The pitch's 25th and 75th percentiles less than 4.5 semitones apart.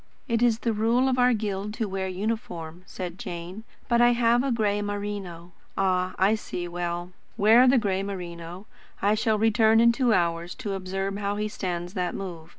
Yes: average, 3.8 semitones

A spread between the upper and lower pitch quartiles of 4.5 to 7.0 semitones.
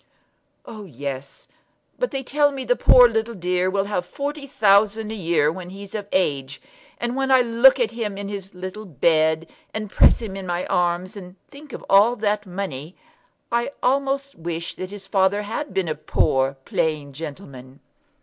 Yes: average, 5.1 semitones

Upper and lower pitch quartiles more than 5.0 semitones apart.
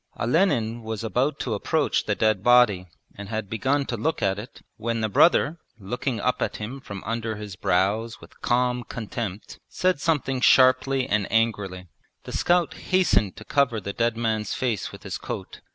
No: average, 3.5 semitones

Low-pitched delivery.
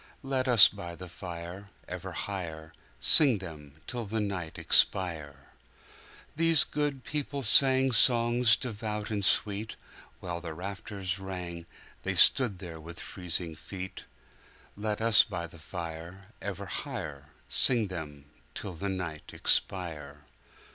Yes: very low, 95 Hz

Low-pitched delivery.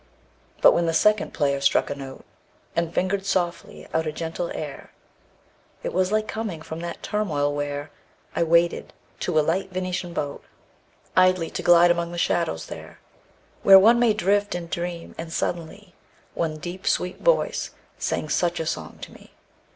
No: medium, 170 Hz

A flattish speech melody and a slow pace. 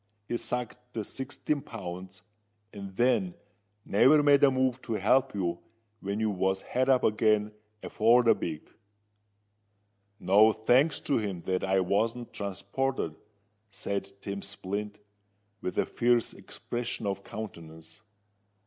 No: average, 4.2 semitones; slow, 130 wpm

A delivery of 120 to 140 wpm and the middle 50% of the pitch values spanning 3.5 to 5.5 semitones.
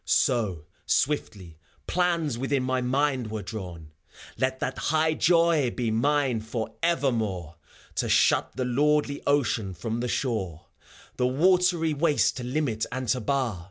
Yes: slow, 135 wpm; average, 5.0 semitones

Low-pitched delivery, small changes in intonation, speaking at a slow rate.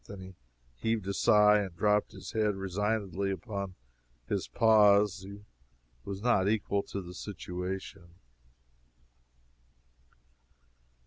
Yes: low, 100 Hz; narrow, 1.8 semitones; slow, 110 wpm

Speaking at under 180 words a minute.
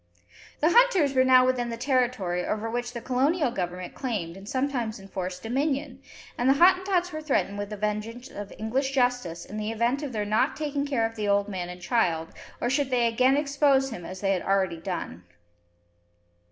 No: average, 195 wpm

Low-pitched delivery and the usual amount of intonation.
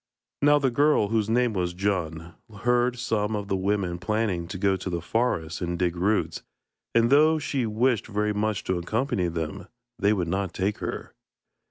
Yes: low, 105 Hz; average, 4.4 semitones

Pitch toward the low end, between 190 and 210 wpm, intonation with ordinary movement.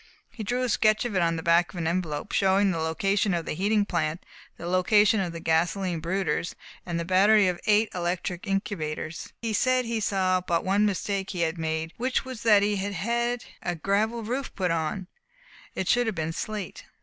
No: high, 190 Hz; fast, 205 wpm; average, 4.0 semitones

